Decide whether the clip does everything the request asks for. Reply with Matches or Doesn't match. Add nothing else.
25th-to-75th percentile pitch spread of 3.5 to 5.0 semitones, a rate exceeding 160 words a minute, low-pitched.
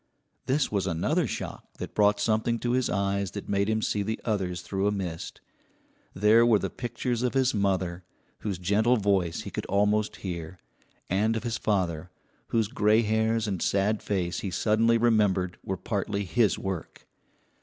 Doesn't match